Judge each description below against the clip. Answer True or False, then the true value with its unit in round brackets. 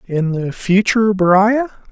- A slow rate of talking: True (125 wpm)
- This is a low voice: False (200 Hz)